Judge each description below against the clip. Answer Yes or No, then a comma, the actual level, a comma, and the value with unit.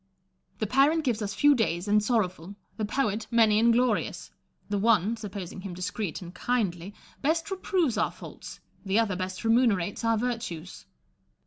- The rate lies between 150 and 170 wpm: Yes, average, 155 wpm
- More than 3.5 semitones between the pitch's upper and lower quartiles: Yes, average, 4.0 semitones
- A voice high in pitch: Yes, high, 215 Hz